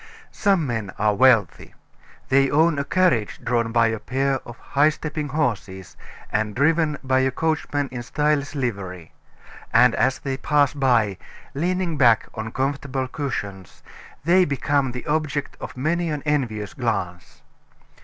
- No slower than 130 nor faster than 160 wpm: Yes, average, 145 wpm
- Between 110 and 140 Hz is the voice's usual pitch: Yes, low, 135 Hz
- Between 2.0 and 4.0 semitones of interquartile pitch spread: No, average, 4.6 semitones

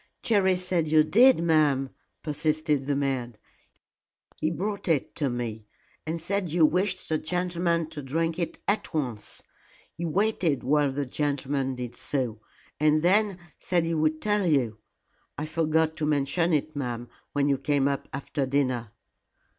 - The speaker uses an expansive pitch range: No, average, 3.7 semitones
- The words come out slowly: No, average, 155 wpm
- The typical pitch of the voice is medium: Yes, medium, 155 Hz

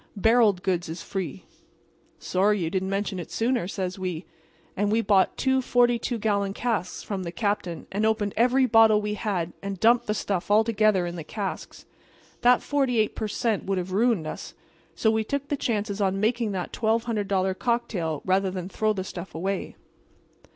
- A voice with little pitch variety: No, average, 3.2 semitones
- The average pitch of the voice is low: No, high, 205 Hz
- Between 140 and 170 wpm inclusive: No, average, 180 wpm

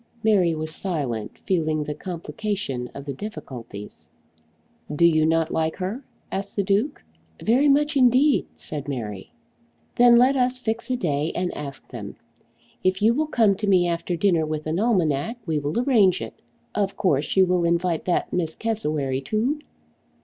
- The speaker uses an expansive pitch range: Yes, wide, 6.3 semitones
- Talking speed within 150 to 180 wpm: Yes, average, 165 wpm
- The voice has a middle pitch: Yes, medium, 180 Hz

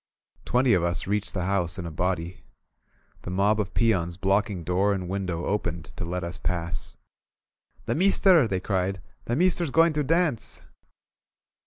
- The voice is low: Yes, very low, 95 Hz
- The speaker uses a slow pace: No, average, 160 wpm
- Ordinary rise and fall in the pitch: Yes, average, 4.7 semitones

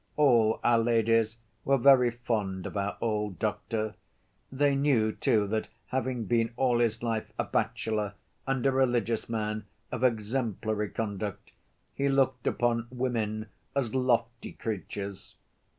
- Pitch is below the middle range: Yes, low, 115 Hz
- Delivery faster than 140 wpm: No, slow, 135 wpm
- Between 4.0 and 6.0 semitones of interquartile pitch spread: No, average, 2.8 semitones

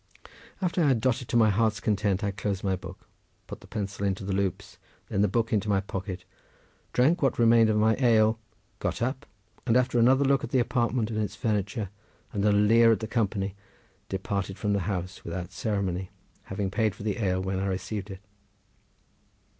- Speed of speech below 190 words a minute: No, average, 195 wpm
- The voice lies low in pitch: Yes, low, 105 Hz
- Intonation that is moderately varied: Yes, average, 3.0 semitones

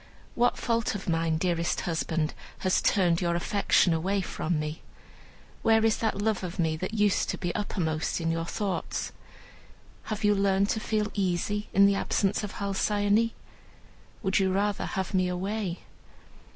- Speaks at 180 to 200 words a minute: No, average, 155 wpm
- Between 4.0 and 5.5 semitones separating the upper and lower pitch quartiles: No, average, 3.2 semitones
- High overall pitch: Yes, high, 195 Hz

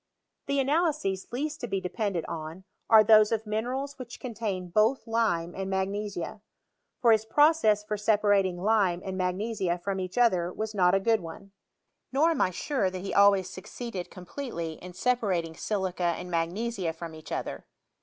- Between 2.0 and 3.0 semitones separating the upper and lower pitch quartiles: No, average, 3.9 semitones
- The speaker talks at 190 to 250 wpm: No, average, 170 wpm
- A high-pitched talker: Yes, high, 200 Hz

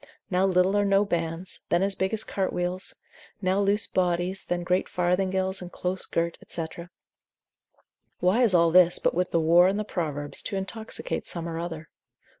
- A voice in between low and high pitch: Yes, medium, 180 Hz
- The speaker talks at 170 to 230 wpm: Yes, average, 180 wpm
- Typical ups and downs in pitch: No, narrow, 2.0 semitones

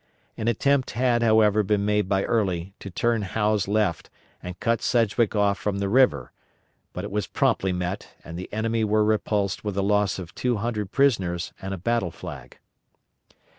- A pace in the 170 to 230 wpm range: Yes, average, 175 wpm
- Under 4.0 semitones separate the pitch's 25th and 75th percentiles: Yes, average, 2.9 semitones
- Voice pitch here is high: No, low, 105 Hz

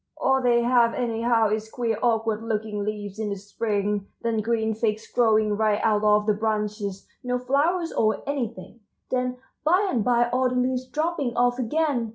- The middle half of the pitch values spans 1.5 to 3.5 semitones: Yes, average, 2.8 semitones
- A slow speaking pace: No, average, 175 wpm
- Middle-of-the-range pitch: No, high, 230 Hz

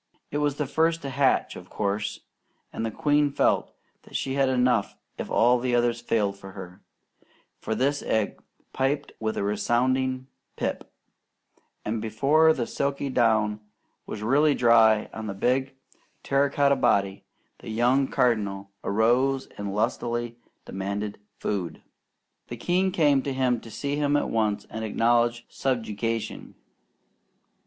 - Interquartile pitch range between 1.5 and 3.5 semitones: No, average, 4.1 semitones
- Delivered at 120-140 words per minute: Yes, slow, 135 wpm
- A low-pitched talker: Yes, low, 120 Hz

